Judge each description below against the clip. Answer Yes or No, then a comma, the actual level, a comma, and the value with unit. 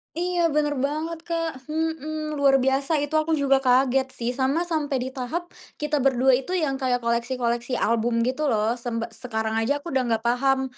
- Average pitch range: Yes, average, 3.7 semitones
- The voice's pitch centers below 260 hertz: No, very high, 270 Hz